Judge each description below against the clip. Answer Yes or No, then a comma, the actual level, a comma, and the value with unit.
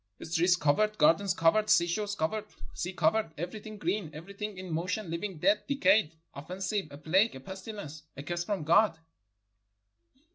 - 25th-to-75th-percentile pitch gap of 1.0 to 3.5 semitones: No, average, 4.3 semitones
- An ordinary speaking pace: Yes, average, 150 wpm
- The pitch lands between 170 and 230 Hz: Yes, medium, 185 Hz